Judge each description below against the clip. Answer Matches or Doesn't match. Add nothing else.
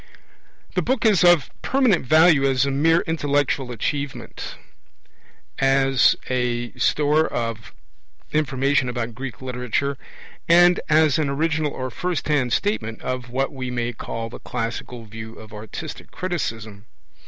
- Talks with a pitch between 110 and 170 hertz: Matches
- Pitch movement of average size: Matches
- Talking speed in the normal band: Doesn't match